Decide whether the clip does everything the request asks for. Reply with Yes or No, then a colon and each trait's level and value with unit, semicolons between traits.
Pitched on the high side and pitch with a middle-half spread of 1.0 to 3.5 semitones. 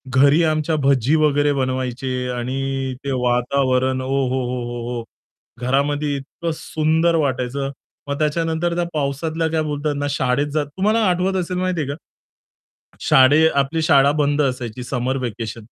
No: medium, 140 Hz; average, 3.1 semitones